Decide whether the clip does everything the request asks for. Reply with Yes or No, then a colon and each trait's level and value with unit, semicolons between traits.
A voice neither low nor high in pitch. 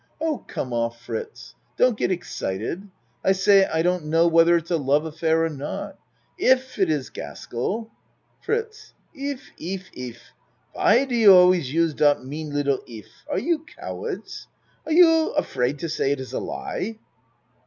Yes: medium, 170 Hz